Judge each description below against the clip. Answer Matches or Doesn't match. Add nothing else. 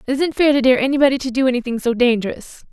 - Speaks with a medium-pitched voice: Doesn't match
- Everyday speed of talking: Doesn't match